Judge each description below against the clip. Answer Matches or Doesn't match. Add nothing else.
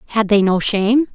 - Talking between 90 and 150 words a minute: Doesn't match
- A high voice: Matches